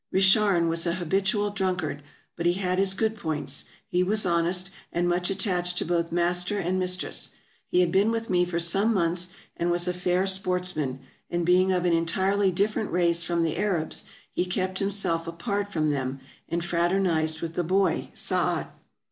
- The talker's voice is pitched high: No, medium, 180 Hz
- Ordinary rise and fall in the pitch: No, narrow, 2.2 semitones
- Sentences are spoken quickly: No, average, 180 wpm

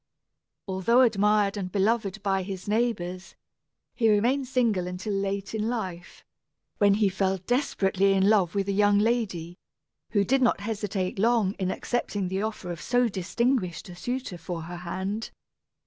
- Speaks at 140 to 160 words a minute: Yes, average, 155 wpm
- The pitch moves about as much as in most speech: Yes, average, 3.1 semitones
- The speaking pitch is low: No, high, 200 Hz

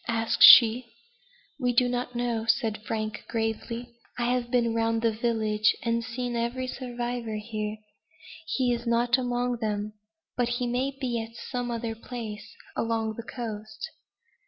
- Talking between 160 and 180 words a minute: No, average, 150 wpm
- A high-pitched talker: Yes, high, 235 Hz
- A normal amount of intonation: No, narrow, 1.7 semitones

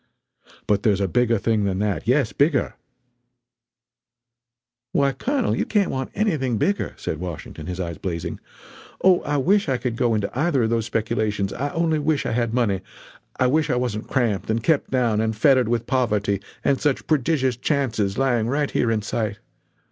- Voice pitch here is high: No, low, 120 Hz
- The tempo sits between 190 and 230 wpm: No, average, 180 wpm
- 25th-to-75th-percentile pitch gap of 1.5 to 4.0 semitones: No, average, 4.5 semitones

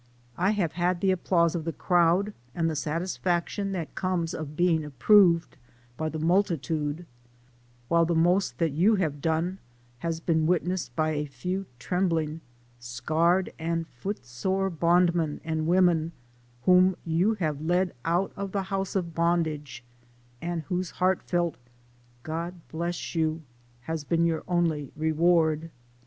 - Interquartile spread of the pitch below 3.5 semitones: Yes, narrow, 2.4 semitones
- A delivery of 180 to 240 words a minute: No, average, 145 wpm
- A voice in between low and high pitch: Yes, medium, 170 Hz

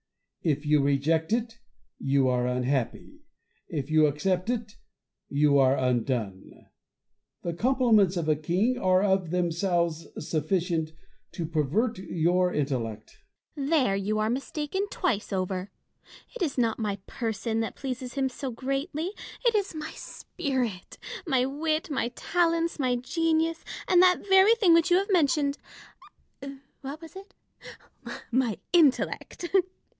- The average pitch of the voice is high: Yes, high, 220 Hz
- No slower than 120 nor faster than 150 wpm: Yes, slow, 135 wpm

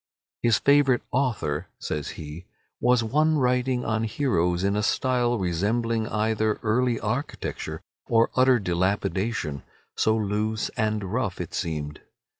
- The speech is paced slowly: Yes, slow, 125 wpm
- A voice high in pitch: No, low, 110 Hz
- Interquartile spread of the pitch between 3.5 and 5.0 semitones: Yes, average, 4.6 semitones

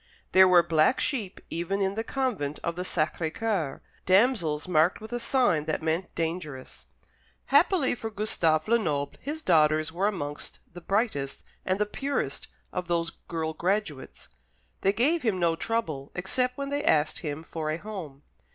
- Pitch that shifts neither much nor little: No, wide, 5.8 semitones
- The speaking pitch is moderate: Yes, medium, 180 Hz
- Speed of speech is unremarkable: Yes, average, 160 wpm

